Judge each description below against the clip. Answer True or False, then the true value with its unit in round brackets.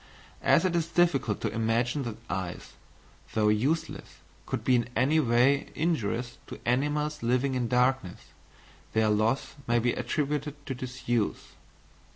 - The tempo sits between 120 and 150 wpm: True (140 wpm)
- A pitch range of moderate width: True (3.9 semitones)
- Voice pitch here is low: True (125 Hz)